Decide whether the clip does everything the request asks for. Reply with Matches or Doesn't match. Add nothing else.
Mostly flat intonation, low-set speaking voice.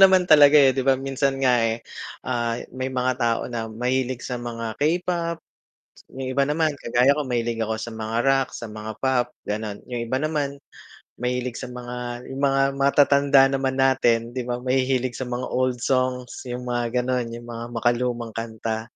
Matches